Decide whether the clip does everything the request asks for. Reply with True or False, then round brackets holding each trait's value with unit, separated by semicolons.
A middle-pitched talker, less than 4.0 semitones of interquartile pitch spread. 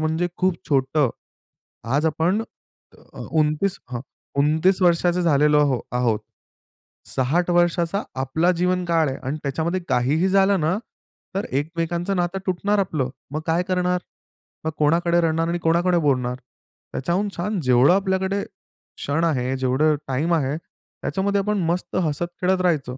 True (165 Hz; 3.6 semitones)